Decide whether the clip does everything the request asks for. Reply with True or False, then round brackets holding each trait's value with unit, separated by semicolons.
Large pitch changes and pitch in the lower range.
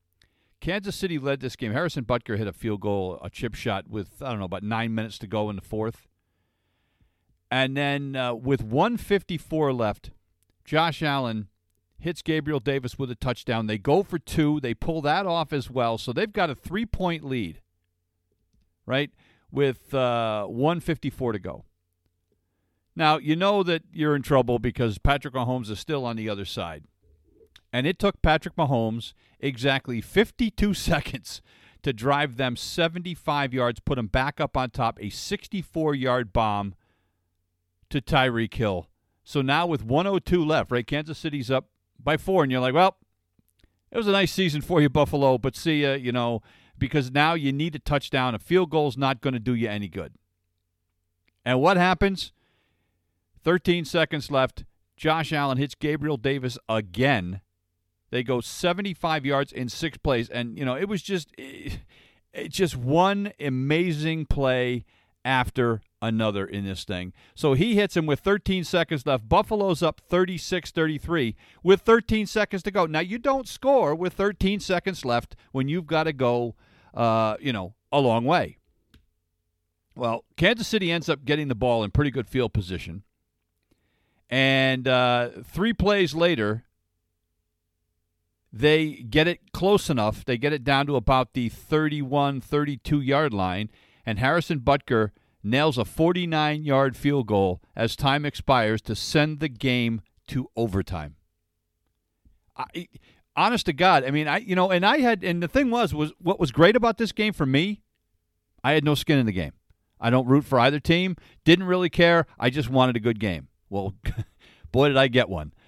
True (7.0 semitones; 130 Hz)